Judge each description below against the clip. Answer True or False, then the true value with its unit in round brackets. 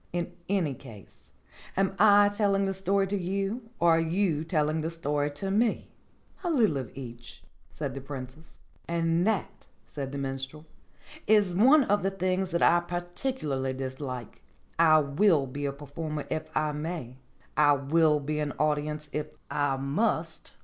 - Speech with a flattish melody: False (5.2 semitones)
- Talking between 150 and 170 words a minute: True (165 wpm)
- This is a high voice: False (160 Hz)